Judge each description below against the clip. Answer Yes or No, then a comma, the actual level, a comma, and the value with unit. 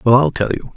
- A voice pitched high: No, low, 105 Hz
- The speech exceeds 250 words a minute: Yes, fast, 315 wpm